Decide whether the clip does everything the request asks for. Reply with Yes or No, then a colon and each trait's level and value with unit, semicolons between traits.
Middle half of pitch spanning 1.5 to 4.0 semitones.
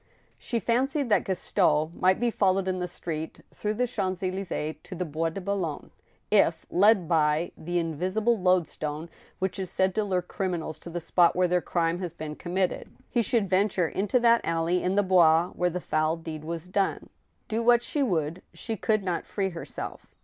Yes: average, 3.3 semitones